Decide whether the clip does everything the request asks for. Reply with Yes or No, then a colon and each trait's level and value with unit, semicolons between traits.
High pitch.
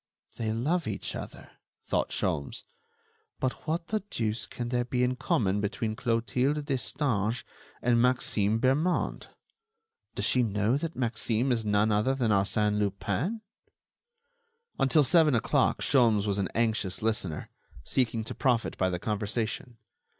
No: low, 115 Hz